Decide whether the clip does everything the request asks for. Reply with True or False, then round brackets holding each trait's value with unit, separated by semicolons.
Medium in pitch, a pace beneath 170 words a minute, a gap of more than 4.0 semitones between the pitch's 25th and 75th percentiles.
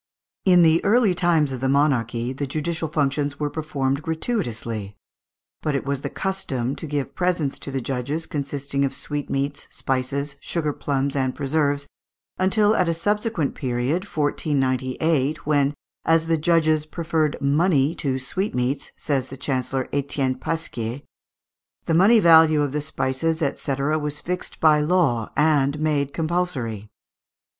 False (145 Hz; 140 wpm; 3.3 semitones)